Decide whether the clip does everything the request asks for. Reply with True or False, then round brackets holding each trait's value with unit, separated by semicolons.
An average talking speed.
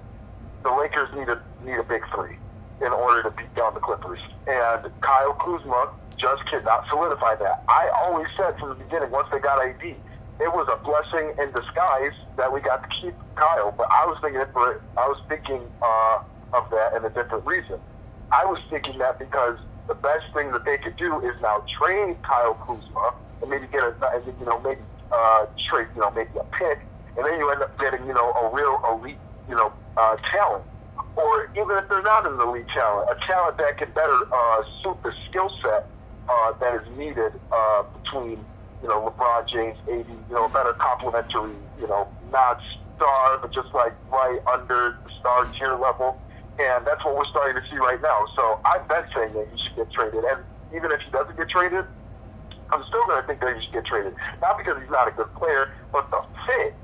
False (210 wpm)